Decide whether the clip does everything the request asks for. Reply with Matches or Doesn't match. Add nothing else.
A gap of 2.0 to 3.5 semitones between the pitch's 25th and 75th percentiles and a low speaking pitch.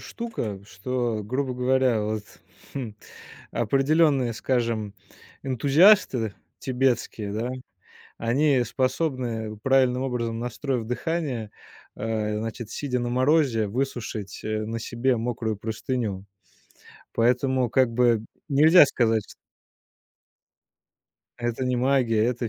Matches